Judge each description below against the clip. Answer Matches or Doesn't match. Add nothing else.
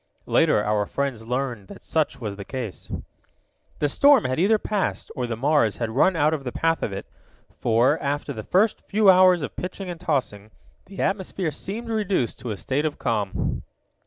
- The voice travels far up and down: Matches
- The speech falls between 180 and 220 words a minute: Matches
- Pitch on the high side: Doesn't match